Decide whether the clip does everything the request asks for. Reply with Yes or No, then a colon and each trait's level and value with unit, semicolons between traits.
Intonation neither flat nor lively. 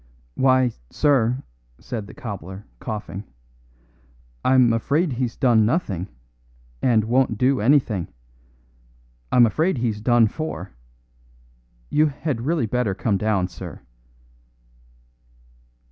Yes: average, 3.9 semitones